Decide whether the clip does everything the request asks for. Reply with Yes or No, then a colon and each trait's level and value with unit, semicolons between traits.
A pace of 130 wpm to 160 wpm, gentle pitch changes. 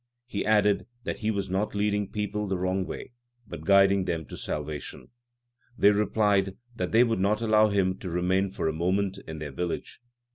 No: average, 185 wpm; narrow, 2.3 semitones